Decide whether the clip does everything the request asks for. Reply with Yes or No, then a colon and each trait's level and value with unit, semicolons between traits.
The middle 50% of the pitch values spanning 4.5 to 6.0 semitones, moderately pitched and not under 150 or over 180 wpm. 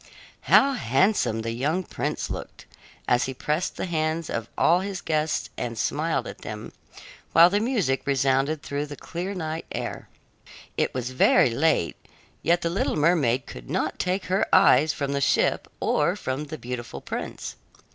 Yes: average, 5.0 semitones; medium, 150 Hz; average, 165 wpm